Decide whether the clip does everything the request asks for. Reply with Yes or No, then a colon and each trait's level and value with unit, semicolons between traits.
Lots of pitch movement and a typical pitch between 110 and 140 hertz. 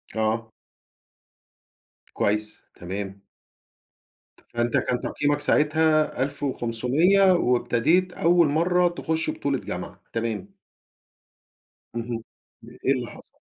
Yes: wide, 5.8 semitones; low, 135 Hz